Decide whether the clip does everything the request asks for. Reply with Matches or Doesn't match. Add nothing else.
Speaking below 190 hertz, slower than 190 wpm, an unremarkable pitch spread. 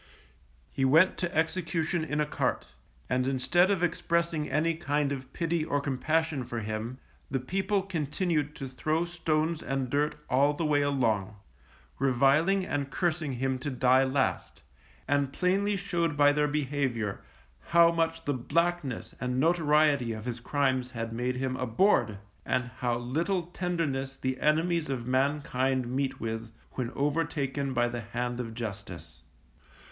Matches